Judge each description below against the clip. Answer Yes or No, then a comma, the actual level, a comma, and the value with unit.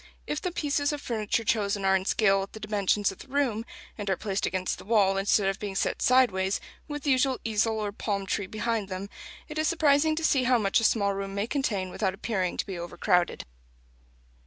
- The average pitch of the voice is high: Yes, high, 210 Hz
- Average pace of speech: No, fast, 215 wpm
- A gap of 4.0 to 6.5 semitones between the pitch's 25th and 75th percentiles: Yes, average, 4.6 semitones